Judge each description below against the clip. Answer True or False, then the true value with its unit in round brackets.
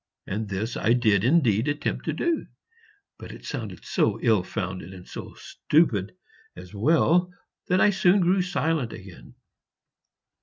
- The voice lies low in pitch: True (120 Hz)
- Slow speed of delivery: False (145 wpm)